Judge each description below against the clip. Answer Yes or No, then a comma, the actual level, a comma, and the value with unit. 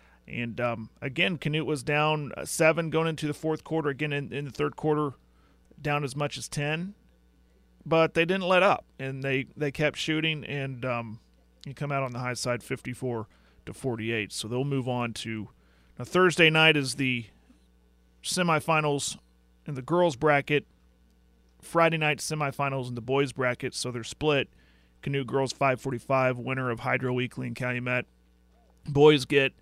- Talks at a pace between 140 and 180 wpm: Yes, average, 165 wpm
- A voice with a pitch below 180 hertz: Yes, low, 135 Hz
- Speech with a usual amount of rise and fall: Yes, average, 4.7 semitones